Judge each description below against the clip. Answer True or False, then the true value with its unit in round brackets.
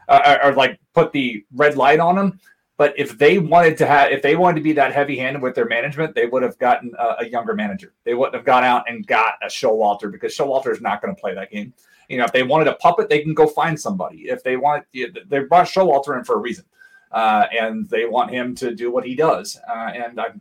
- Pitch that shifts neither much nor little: False (6.0 semitones)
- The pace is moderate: False (255 wpm)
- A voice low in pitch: False (145 Hz)